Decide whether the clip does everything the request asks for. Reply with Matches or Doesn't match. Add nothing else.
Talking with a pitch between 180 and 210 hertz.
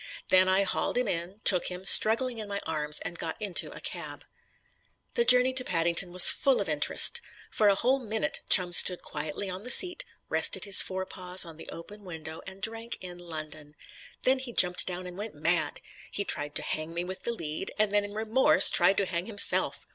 Matches